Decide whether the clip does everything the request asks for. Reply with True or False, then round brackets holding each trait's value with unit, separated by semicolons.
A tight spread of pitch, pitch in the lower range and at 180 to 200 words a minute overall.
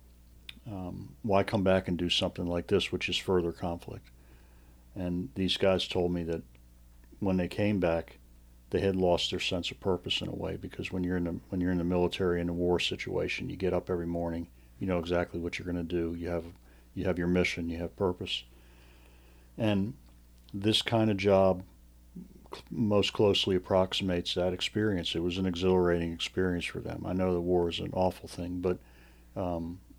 True (2.2 semitones; 90 Hz; 195 wpm)